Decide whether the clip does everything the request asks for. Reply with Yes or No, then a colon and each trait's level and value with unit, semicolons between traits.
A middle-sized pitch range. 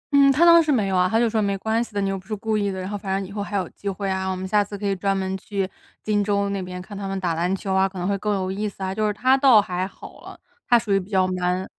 No: narrow, 2.0 semitones